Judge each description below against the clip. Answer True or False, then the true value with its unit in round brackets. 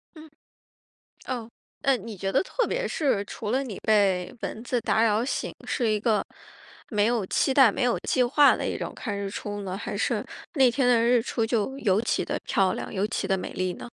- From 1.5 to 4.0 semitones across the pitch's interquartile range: True (3.7 semitones)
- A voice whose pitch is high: True (225 Hz)